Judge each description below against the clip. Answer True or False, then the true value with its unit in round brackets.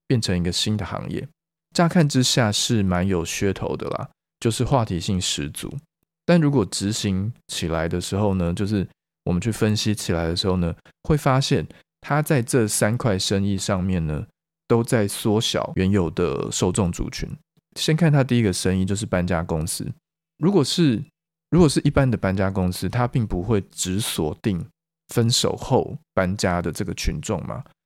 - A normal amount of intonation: False (7.5 semitones)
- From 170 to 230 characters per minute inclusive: False (255 characters per minute)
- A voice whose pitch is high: False (110 Hz)